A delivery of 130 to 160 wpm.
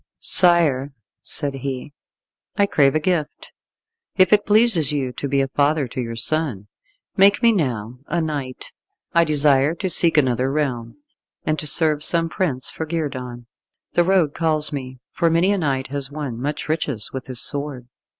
No: average, 170 wpm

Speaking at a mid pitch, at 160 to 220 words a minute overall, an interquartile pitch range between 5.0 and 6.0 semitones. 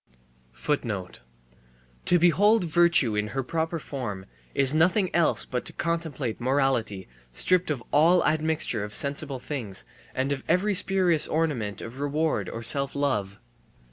No: medium, 145 Hz; slow, 135 wpm; average, 5.3 semitones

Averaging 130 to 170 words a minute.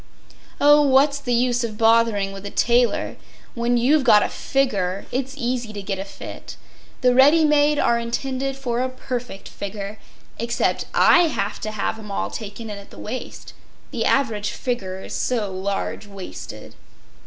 Yes: average, 155 wpm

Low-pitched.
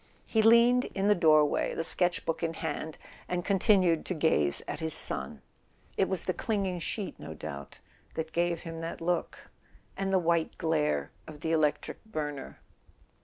No: medium, 165 Hz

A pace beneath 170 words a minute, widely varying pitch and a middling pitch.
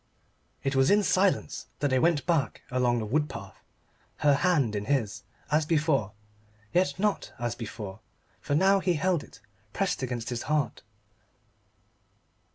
Yes: average, 150 wpm; wide, 6.2 semitones; medium, 145 Hz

